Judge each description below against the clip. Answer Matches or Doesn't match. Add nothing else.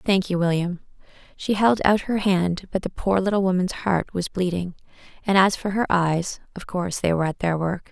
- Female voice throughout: Matches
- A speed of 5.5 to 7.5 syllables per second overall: Doesn't match